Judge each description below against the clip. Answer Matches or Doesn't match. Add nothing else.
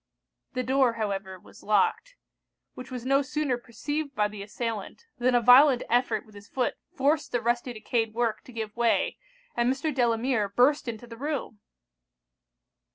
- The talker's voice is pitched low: Doesn't match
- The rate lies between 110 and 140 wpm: Doesn't match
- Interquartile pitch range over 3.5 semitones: Doesn't match